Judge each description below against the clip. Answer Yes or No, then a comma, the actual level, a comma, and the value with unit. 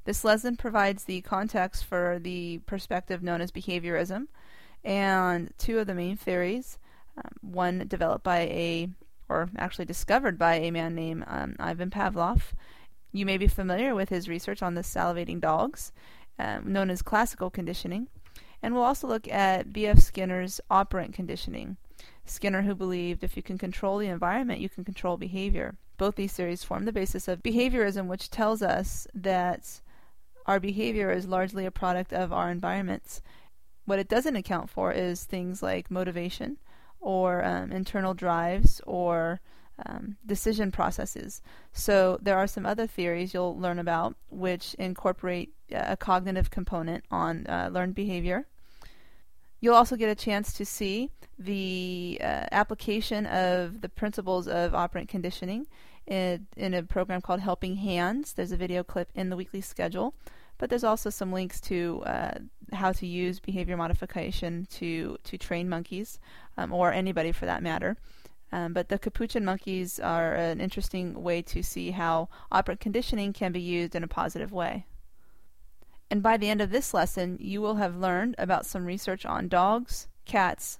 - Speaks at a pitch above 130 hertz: Yes, medium, 185 Hz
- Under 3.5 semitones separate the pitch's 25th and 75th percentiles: Yes, narrow, 2.5 semitones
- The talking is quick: No, average, 160 wpm